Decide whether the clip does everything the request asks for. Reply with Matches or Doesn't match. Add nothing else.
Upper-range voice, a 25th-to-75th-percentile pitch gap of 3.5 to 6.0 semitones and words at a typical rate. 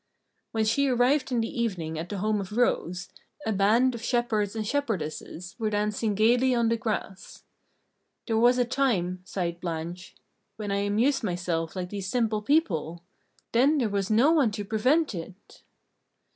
Matches